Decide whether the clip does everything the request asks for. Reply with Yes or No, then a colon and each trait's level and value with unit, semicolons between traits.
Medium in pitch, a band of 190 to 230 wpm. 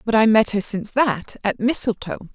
No: high, 220 Hz; fast, 205 wpm